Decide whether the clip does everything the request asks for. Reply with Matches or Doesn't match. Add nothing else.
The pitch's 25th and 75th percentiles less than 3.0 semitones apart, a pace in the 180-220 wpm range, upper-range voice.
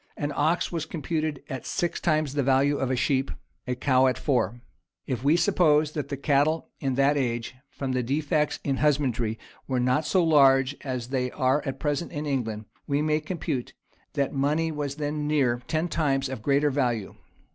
Doesn't match